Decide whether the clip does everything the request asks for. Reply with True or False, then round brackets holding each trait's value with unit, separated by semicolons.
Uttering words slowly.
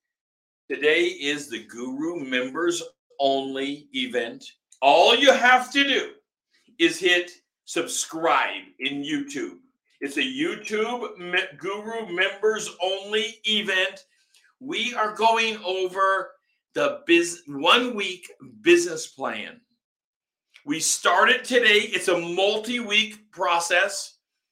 True (105 wpm)